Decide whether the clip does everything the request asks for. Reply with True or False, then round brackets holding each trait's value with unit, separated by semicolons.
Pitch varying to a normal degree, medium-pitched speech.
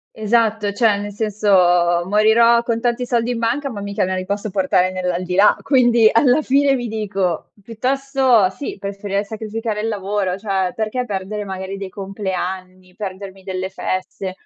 False (3.3 semitones; 205 Hz)